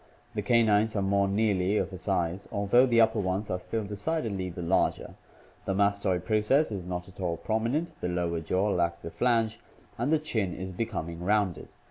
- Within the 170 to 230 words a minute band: Yes, average, 185 wpm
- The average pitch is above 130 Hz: No, low, 100 Hz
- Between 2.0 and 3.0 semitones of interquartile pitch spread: No, average, 3.4 semitones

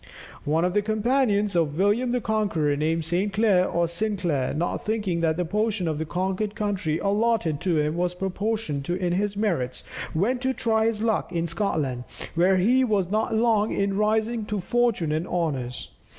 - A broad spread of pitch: No, average, 4.5 semitones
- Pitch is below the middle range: No, high, 195 Hz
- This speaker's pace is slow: No, average, 180 wpm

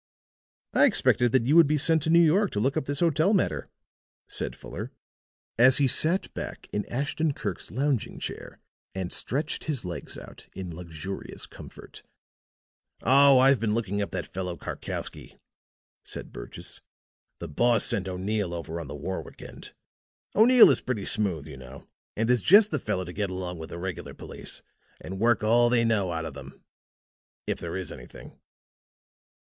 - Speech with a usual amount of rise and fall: No, wide, 7.4 semitones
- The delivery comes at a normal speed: Yes, average, 170 wpm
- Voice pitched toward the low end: Yes, low, 110 Hz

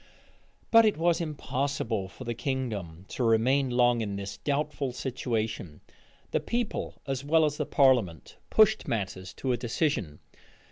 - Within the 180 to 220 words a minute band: No, average, 145 wpm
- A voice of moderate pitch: No, low, 125 Hz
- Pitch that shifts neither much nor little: Yes, average, 5.0 semitones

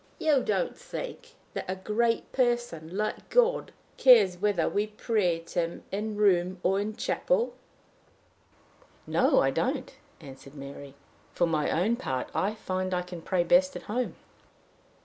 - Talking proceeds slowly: No, average, 160 wpm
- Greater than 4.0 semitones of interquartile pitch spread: Yes, average, 5.2 semitones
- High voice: Yes, high, 200 Hz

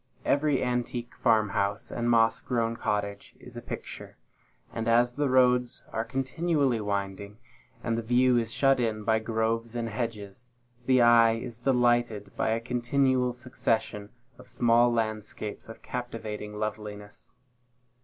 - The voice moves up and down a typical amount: No, narrow, 2.2 semitones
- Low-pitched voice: Yes, low, 115 Hz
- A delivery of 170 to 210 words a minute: No, average, 140 wpm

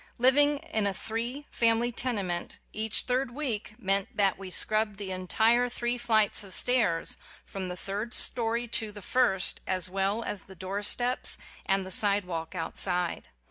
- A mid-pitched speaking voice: No, high, 210 Hz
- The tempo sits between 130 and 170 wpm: Yes, average, 165 wpm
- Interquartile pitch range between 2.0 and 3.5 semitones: No, average, 3.9 semitones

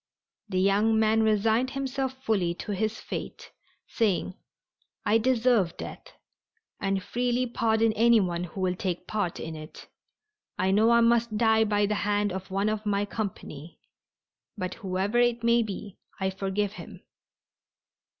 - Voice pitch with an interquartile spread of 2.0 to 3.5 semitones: Yes, average, 3.1 semitones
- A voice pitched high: Yes, high, 210 Hz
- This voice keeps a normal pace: Yes, average, 145 wpm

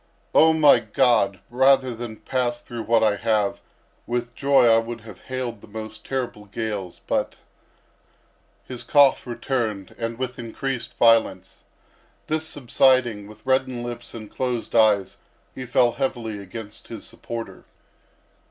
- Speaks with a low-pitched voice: Yes, low, 120 Hz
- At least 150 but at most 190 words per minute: No, slow, 135 wpm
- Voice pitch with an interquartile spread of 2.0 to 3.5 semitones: Yes, average, 2.8 semitones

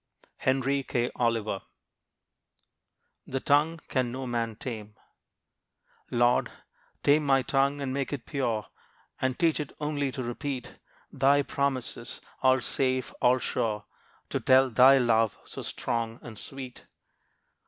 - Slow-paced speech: Yes, slow, 125 wpm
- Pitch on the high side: No, low, 130 Hz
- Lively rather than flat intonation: No, narrow, 2.6 semitones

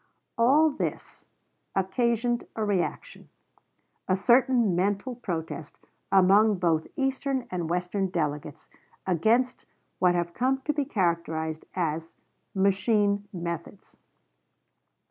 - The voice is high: Yes, high, 195 Hz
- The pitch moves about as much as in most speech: No, wide, 5.7 semitones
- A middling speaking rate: No, slow, 100 wpm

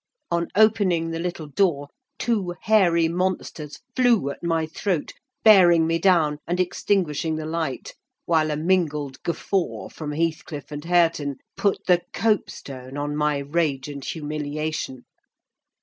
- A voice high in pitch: No, medium, 165 Hz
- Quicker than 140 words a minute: No, slow, 135 wpm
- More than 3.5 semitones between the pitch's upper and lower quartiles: No, average, 3.1 semitones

